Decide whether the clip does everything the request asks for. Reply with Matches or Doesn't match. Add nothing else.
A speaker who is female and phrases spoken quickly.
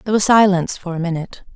Matches